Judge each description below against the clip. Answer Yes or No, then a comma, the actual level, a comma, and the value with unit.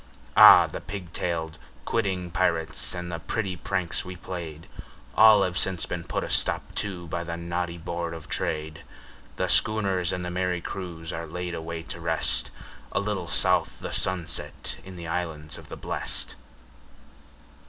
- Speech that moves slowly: No, average, 165 wpm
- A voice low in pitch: Yes, very low, 85 Hz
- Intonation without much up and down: Yes, narrow, 1.9 semitones